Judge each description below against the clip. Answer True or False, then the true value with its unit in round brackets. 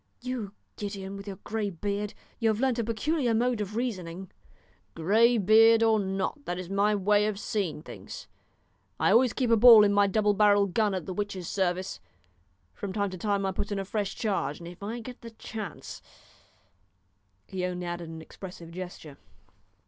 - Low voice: False (205 Hz)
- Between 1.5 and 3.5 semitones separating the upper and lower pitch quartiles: True (3.0 semitones)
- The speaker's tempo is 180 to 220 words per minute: True (185 wpm)